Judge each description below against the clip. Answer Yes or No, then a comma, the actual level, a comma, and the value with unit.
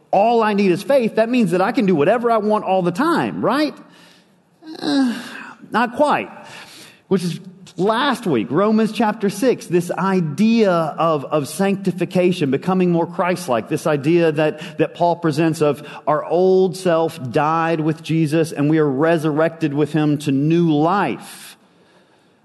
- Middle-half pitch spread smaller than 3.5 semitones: No, average, 5.1 semitones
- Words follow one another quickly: No, average, 160 wpm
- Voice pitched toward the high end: No, medium, 175 Hz